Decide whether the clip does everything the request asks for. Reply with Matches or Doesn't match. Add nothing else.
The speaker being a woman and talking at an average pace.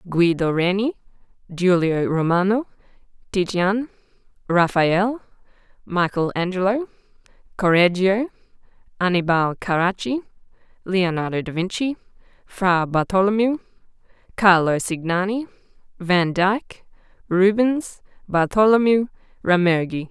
Doesn't match